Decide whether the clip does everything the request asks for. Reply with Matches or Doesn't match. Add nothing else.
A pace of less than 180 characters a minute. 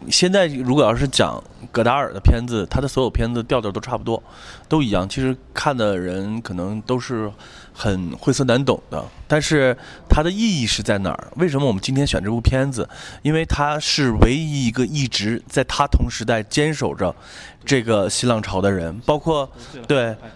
Doesn't match